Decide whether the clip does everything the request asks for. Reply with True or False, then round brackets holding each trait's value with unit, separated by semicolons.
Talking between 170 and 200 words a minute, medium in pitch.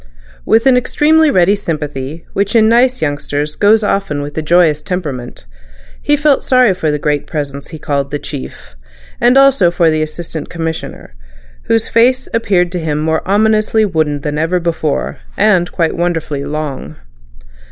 False (160 wpm; 170 Hz)